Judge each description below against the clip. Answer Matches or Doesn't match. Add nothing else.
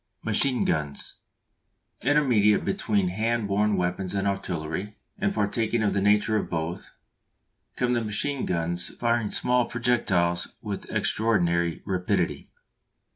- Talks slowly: Matches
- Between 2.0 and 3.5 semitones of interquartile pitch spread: Doesn't match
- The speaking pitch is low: Matches